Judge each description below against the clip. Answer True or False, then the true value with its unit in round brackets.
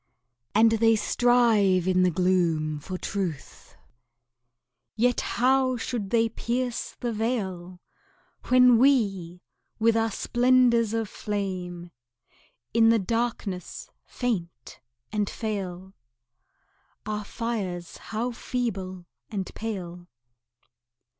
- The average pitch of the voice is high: True (215 Hz)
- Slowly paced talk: True (95 wpm)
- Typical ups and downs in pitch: True (4.3 semitones)